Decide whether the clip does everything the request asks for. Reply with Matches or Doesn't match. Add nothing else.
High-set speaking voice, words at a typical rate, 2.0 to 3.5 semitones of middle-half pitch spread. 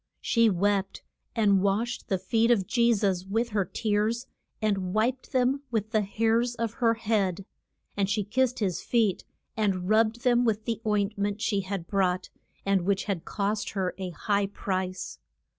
Matches